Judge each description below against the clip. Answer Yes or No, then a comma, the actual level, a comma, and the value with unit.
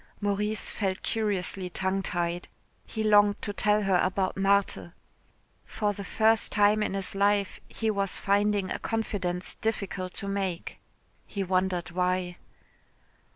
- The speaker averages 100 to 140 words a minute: Yes, slow, 135 wpm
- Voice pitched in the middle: No, high, 195 Hz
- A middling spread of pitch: No, narrow, 2.0 semitones